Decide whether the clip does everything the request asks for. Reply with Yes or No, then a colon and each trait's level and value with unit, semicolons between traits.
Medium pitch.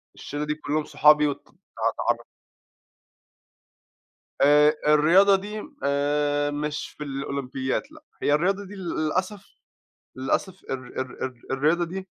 Yes: medium, 150 Hz